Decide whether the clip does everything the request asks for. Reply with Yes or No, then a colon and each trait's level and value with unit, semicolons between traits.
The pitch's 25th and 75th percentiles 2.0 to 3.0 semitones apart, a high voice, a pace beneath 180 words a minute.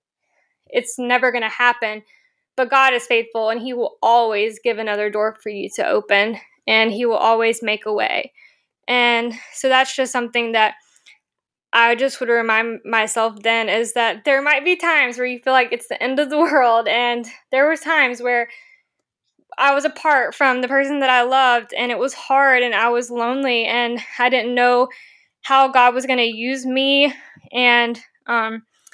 No: average, 2.7 semitones; high, 245 Hz; average, 185 wpm